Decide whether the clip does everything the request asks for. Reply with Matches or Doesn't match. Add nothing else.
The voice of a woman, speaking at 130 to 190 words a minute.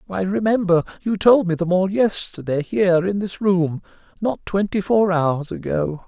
Doesn't match